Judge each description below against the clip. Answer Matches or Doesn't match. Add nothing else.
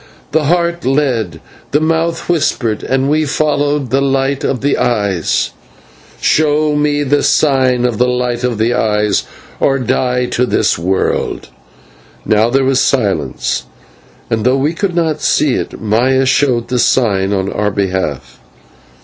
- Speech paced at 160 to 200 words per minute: Doesn't match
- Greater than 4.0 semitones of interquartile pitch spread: Matches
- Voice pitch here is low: Matches